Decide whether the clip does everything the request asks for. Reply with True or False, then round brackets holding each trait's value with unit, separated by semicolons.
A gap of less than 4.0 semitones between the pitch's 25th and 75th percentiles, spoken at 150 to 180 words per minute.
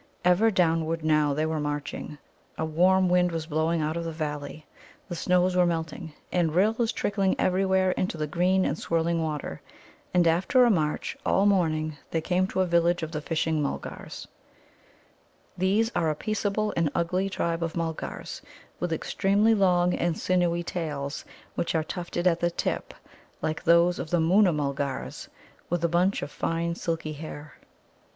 True (2.6 semitones; 165 wpm)